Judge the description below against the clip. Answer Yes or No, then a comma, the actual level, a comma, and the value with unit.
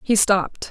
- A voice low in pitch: No, high, 200 Hz